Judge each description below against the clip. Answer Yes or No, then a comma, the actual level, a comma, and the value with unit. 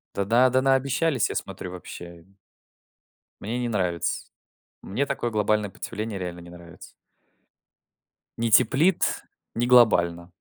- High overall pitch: No, low, 105 Hz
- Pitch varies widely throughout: Yes, wide, 6.0 semitones